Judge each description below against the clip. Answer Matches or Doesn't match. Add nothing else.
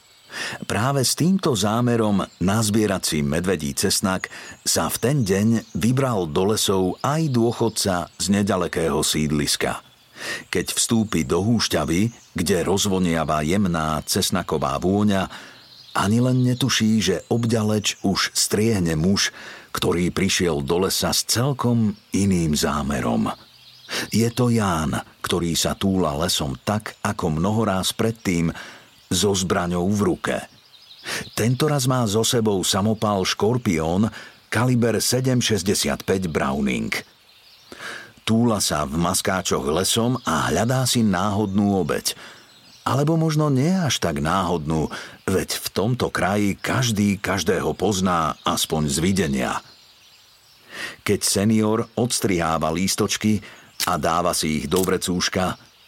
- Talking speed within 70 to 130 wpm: Matches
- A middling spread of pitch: Matches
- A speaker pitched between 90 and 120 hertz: Matches